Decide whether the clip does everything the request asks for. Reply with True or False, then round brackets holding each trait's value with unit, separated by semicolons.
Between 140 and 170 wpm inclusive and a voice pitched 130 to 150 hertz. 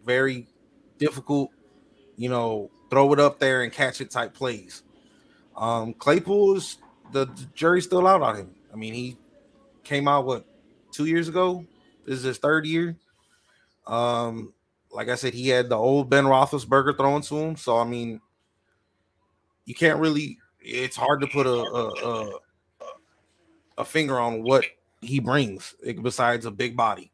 True (160 wpm; 135 Hz)